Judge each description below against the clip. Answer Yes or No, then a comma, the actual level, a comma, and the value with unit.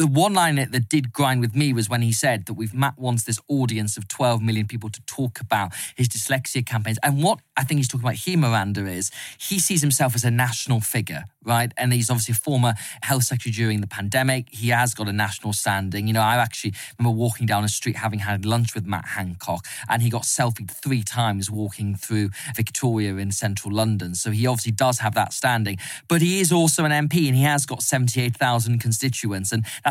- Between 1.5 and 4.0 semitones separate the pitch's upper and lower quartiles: Yes, average, 3.3 semitones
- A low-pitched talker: Yes, low, 120 Hz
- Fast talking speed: Yes, fast, 220 wpm